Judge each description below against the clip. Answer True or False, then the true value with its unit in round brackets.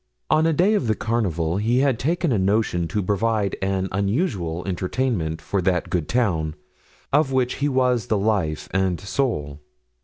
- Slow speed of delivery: False (165 wpm)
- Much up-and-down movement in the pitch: True (6.0 semitones)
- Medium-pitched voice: False (105 Hz)